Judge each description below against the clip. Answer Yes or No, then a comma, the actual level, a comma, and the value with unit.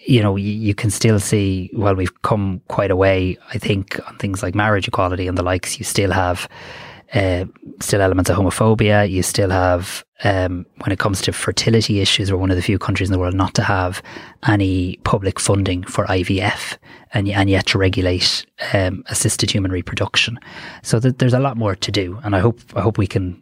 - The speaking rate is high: Yes, fast, 215 wpm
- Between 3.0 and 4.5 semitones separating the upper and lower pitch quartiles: No, narrow, 2.5 semitones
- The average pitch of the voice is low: Yes, low, 100 Hz